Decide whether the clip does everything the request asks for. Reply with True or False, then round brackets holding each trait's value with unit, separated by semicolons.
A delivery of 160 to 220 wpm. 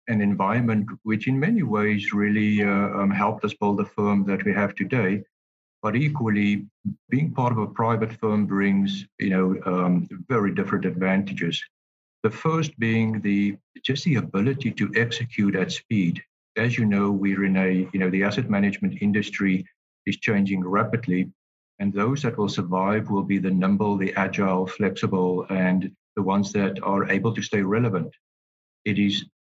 True (165 wpm)